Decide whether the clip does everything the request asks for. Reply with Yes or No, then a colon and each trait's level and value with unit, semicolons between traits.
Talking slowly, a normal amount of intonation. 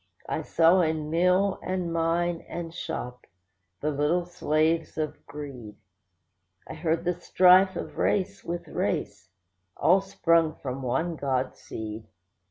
Yes: slow, 130 wpm; average, 3.0 semitones